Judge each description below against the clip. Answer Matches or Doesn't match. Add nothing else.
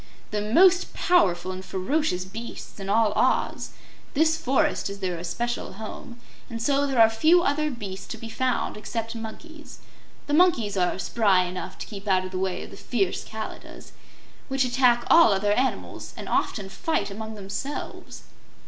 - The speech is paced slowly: Doesn't match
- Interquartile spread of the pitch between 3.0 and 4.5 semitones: Doesn't match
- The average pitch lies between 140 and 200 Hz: Doesn't match